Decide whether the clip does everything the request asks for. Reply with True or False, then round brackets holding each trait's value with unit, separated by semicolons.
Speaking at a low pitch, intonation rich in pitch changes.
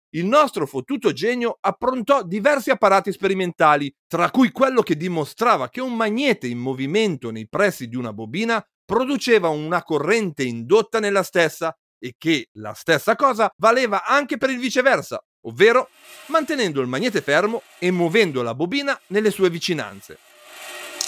False (195 Hz; 7.6 semitones)